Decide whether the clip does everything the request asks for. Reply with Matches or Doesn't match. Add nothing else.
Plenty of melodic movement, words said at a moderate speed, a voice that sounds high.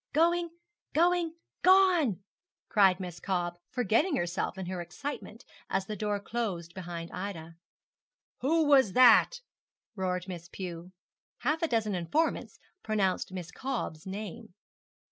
Doesn't match